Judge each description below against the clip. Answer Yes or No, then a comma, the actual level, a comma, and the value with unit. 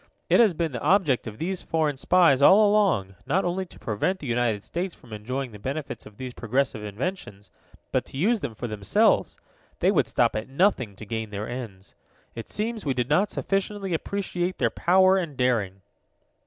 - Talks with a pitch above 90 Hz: Yes, low, 135 Hz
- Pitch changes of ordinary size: No, wide, 8.8 semitones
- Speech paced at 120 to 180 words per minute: No, average, 190 wpm